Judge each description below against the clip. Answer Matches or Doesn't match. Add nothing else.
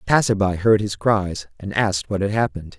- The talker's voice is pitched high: Doesn't match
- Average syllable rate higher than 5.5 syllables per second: Matches